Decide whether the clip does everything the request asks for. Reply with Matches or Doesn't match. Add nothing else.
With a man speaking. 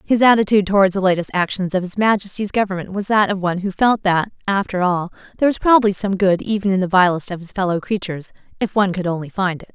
Doesn't match